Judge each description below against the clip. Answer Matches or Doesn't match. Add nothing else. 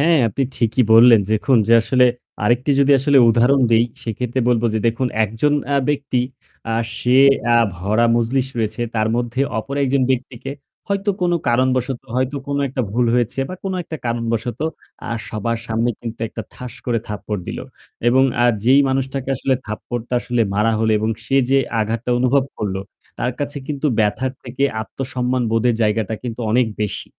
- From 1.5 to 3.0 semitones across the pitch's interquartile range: Matches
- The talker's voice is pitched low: Matches